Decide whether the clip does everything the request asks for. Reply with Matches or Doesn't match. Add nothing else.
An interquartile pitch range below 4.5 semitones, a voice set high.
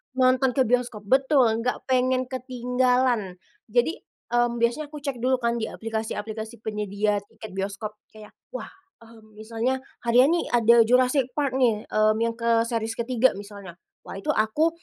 Matches